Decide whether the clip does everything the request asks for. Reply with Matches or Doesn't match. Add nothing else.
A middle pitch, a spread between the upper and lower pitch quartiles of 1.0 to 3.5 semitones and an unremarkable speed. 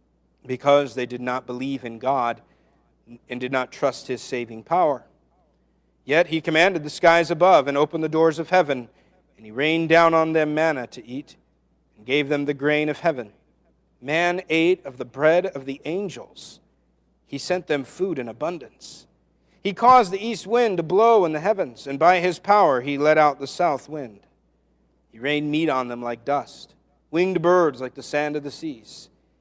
Doesn't match